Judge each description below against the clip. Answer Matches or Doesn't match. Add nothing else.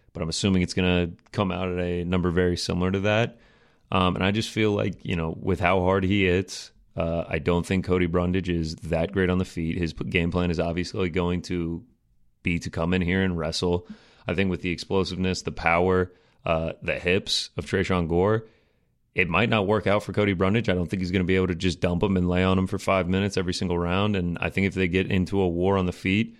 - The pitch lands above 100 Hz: Doesn't match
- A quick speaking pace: Matches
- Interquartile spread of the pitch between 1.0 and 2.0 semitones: Matches